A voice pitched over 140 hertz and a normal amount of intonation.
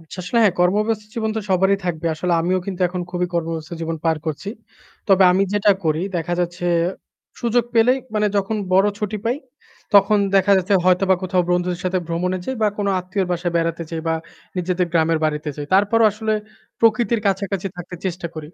Yes: medium, 185 Hz; average, 3.2 semitones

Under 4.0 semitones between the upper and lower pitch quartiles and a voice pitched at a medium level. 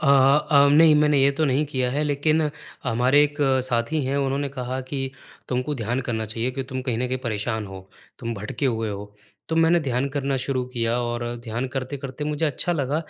No: average, 3.3 semitones; low, 130 Hz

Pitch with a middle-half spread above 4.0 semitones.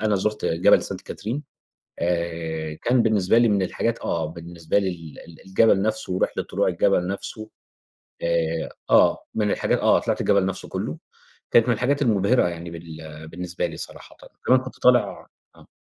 Yes: average, 4.6 semitones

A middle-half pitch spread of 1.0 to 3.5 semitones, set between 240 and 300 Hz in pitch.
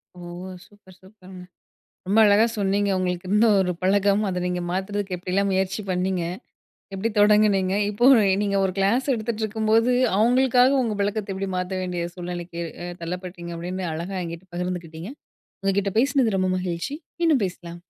No: average, 2.8 semitones; high, 190 Hz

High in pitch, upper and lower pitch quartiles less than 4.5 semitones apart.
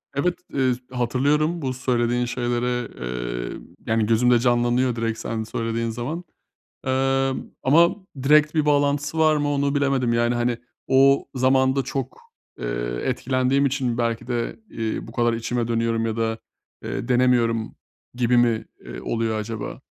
No: low, 125 Hz; narrow, 2.6 semitones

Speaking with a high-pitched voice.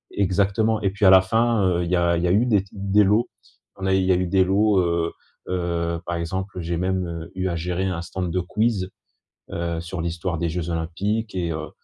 No: very low, 90 Hz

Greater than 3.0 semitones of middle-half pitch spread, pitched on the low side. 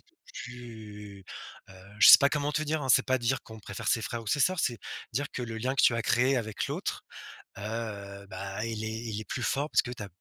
Yes: average, 3.8 semitones; low, 115 Hz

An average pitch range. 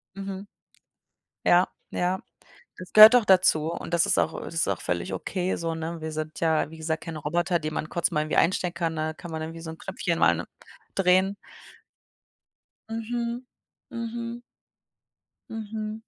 Yes: average, 4.2 semitones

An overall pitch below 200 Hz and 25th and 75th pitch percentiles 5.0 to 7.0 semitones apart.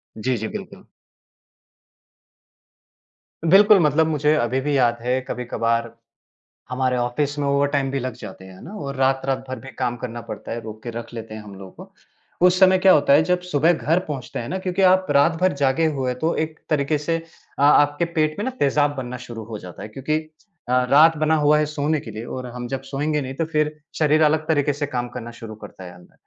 No: medium, 140 Hz; average, 4.2 semitones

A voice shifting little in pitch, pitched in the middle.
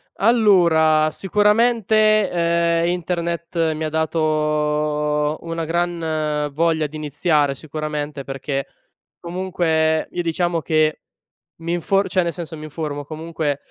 Yes: narrow, 2.2 semitones; medium, 160 Hz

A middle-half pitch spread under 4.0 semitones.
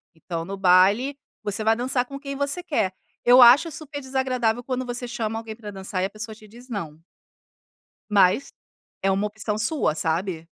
No: average, 4.8 semitones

